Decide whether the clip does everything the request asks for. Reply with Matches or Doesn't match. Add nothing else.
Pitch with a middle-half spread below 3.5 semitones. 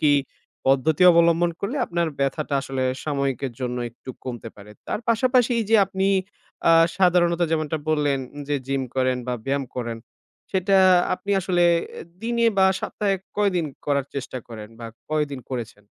Doesn't match